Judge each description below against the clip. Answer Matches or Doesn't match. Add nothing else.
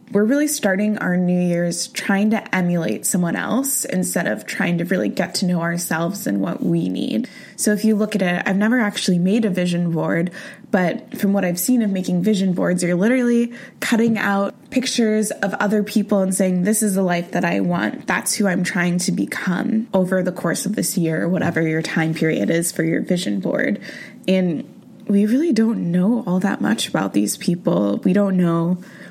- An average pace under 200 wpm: Doesn't match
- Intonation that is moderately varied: Matches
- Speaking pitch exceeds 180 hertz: Matches